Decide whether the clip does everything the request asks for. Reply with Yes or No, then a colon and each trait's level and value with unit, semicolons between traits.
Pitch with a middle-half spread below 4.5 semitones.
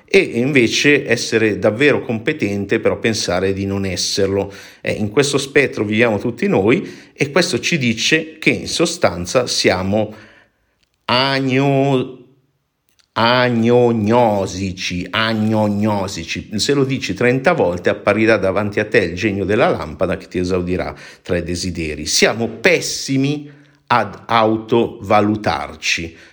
No: wide, 5.5 semitones